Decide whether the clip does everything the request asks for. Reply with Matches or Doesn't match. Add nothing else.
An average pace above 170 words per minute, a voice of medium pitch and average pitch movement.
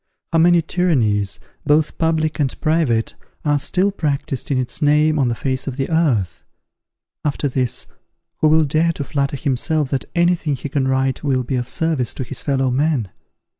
Matches